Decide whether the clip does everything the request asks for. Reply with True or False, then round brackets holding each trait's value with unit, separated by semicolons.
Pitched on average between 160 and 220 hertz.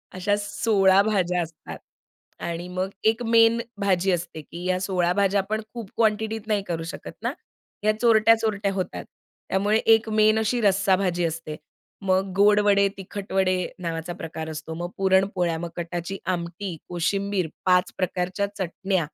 True (190 Hz)